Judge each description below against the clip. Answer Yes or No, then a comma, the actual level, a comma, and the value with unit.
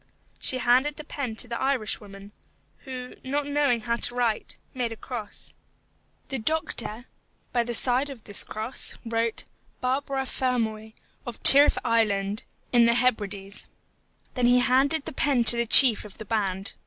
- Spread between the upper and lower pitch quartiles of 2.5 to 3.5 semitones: Yes, average, 3.1 semitones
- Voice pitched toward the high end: Yes, high, 240 Hz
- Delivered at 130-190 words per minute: Yes, average, 160 wpm